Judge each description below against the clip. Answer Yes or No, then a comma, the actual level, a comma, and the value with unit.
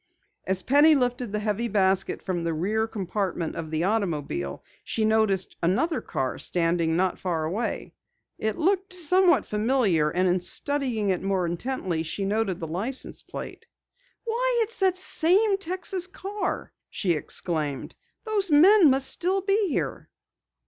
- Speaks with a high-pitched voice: Yes, high, 220 Hz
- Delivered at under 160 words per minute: Yes, average, 145 wpm